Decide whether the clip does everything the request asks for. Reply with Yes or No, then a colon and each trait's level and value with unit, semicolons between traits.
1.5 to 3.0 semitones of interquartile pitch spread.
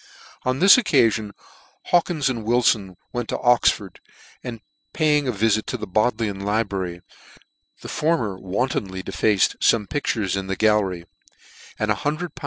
No: average, 4.5 semitones